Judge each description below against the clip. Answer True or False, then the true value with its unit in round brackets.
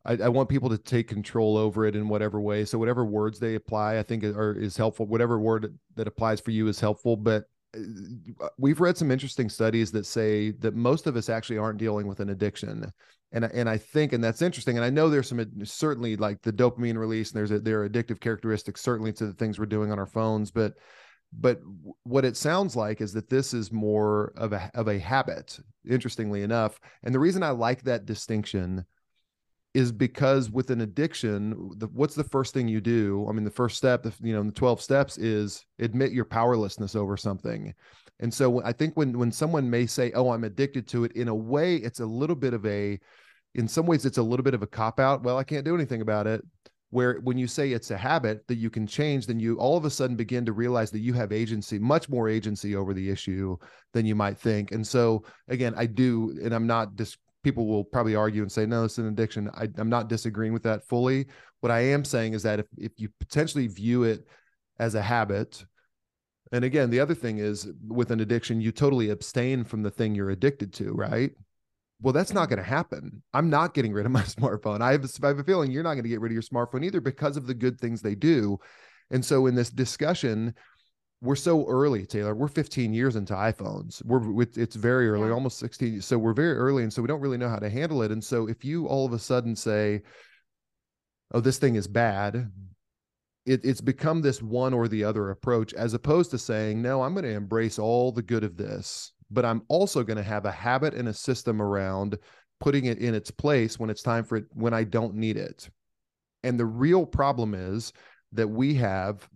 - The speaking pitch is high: False (115 Hz)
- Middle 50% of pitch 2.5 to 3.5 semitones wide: True (3.1 semitones)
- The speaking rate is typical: False (225 wpm)